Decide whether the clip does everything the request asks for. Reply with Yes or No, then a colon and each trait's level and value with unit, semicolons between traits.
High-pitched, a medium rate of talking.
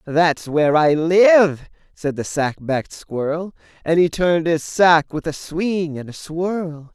No: medium, 165 Hz; average, 175 wpm